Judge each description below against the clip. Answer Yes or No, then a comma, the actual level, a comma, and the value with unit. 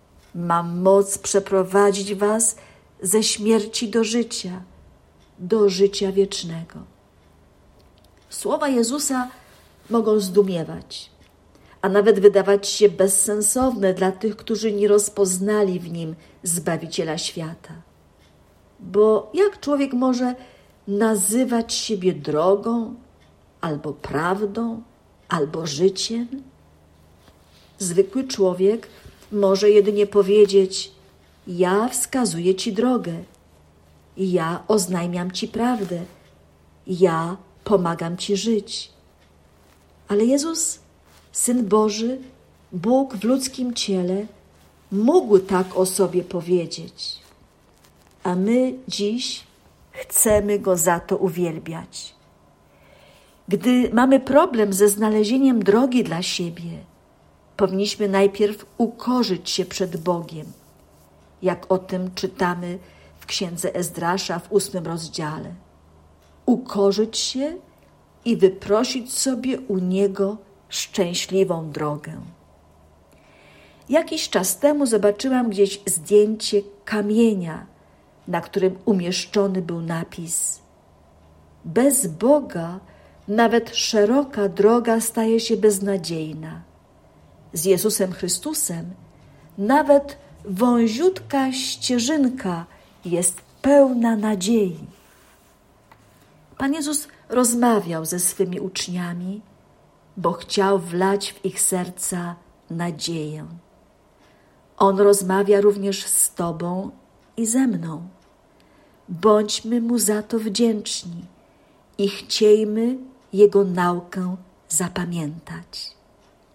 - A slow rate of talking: Yes, slow, 90 wpm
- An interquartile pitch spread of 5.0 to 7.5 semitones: No, average, 4.3 semitones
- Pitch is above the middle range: Yes, high, 195 Hz